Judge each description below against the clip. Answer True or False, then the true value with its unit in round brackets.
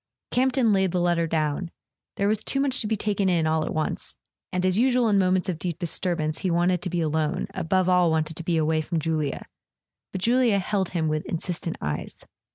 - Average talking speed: False (210 wpm)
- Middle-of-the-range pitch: True (180 Hz)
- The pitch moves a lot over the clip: False (3.6 semitones)